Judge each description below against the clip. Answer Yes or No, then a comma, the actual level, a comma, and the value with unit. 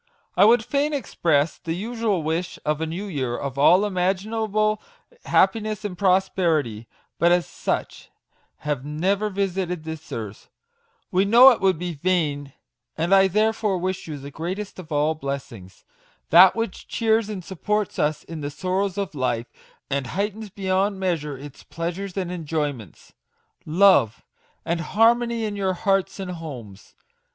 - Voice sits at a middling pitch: Yes, medium, 180 Hz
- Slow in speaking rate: No, average, 150 wpm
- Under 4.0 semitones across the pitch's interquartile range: No, average, 4.8 semitones